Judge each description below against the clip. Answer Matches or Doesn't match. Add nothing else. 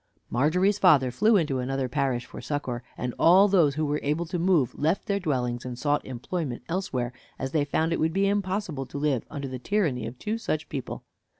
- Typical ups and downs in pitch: Doesn't match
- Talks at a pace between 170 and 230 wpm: Matches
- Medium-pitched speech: Matches